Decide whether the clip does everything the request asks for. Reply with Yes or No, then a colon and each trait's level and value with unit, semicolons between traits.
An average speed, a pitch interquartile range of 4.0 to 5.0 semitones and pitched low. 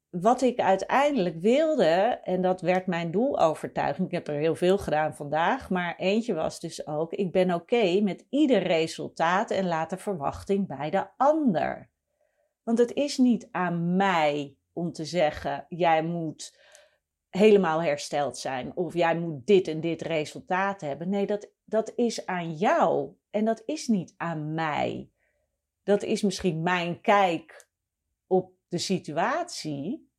No: average, 155 wpm; average, 4.3 semitones; medium, 185 Hz